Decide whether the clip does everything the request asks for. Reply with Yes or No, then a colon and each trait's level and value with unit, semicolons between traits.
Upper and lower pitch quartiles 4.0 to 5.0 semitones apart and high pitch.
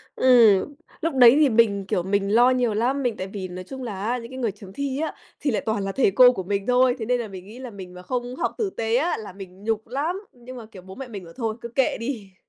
Yes: average, 4.3 semitones; high, 230 Hz